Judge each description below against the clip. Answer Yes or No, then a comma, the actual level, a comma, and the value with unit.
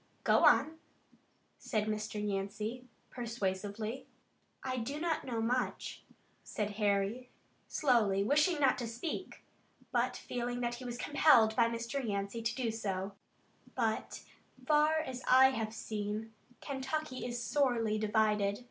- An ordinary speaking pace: No, slow, 130 wpm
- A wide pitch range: No, average, 3.4 semitones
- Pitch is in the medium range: No, high, 230 Hz